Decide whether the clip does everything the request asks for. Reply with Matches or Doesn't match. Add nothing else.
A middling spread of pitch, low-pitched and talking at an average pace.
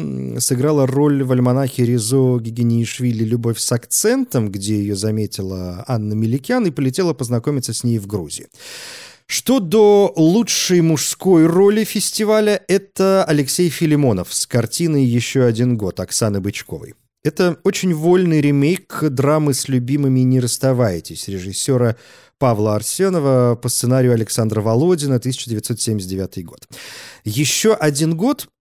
Doesn't match